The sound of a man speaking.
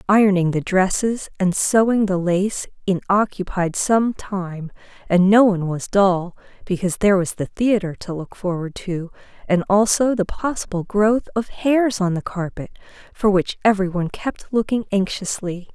No: female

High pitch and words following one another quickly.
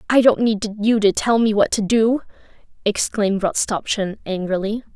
No: high, 210 Hz; average, 155 wpm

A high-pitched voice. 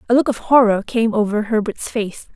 Yes: high, 225 Hz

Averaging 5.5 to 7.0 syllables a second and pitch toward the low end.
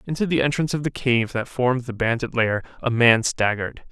Yes: 5.9 syllables/s; low, 125 Hz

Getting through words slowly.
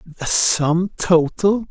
Yes: slow, 105 wpm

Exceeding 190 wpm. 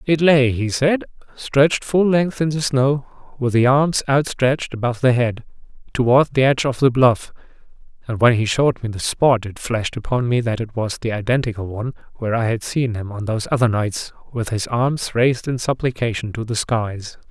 Yes: average, 200 wpm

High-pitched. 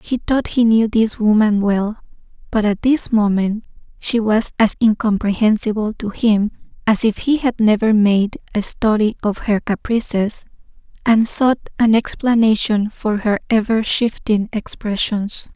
Yes: high, 215 Hz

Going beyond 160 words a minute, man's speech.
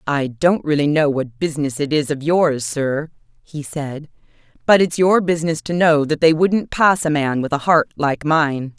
No: fast, 205 wpm; female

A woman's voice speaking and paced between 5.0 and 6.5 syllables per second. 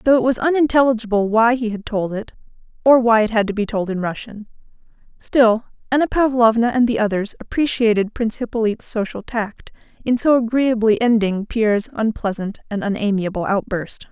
Yes: female; 5.4 syllables/s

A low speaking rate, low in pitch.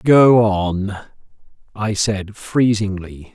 Yes: slow, 90 wpm; low, 105 Hz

